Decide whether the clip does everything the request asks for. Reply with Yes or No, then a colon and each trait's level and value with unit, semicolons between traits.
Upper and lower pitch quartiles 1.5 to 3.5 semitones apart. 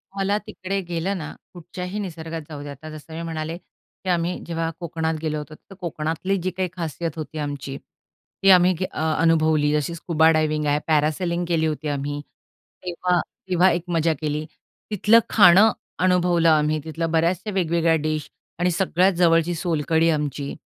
Yes: narrow, 2.5 semitones